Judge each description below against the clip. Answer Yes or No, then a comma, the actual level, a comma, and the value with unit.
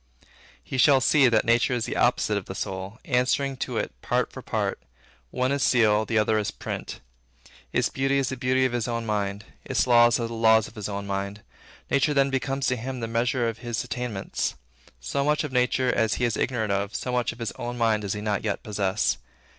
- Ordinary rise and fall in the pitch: Yes, average, 3.2 semitones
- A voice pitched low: Yes, low, 115 Hz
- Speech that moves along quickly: Yes, fast, 220 wpm